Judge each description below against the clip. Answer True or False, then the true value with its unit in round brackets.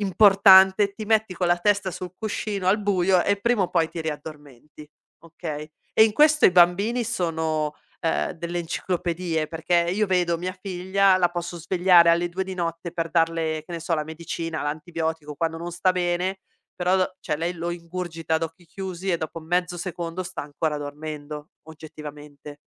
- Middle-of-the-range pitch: True (175 Hz)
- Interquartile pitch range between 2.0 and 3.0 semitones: True (2.5 semitones)